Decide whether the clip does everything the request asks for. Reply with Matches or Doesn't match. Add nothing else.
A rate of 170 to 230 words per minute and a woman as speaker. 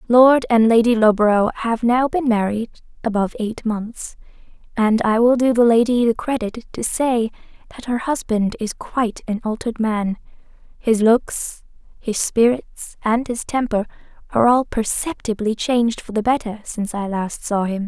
Doesn't match